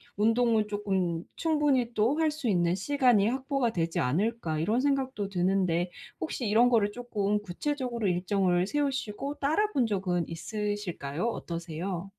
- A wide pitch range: Yes, wide, 5.7 semitones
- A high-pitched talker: Yes, high, 210 Hz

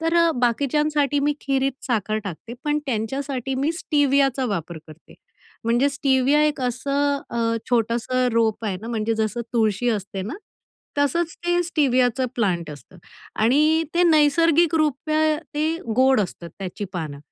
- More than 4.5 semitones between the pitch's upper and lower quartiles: Yes, average, 4.9 semitones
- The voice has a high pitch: Yes, very high, 260 Hz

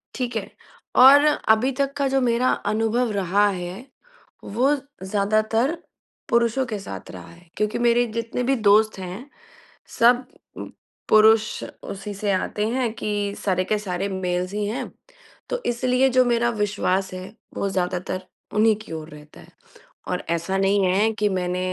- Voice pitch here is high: Yes, high, 215 Hz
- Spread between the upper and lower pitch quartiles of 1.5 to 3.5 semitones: No, average, 4.1 semitones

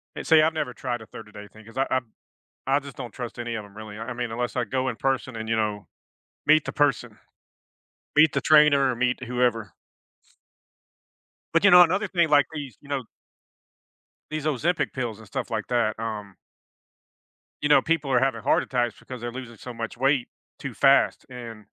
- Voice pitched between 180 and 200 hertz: No, low, 125 Hz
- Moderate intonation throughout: Yes, average, 4.0 semitones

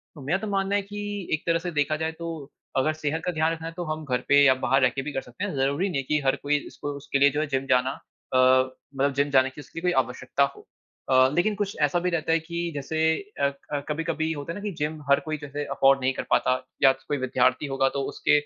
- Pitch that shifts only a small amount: No, average, 3.6 semitones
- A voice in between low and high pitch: Yes, medium, 145 Hz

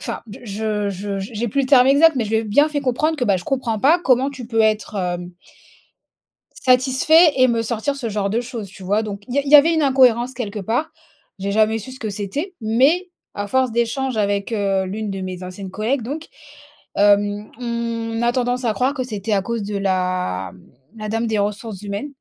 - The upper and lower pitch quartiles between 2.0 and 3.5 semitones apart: No, average, 4.2 semitones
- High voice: Yes, high, 225 Hz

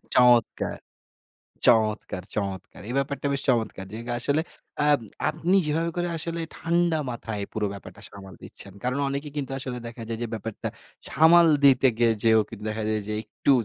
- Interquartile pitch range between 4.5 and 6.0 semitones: Yes, average, 5.2 semitones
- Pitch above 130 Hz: No, low, 125 Hz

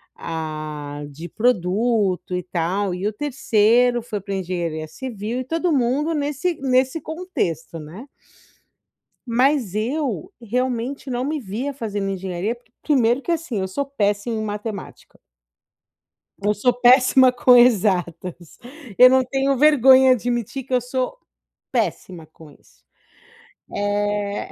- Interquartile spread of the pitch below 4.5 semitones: No, average, 5.2 semitones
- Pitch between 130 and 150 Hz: No, high, 230 Hz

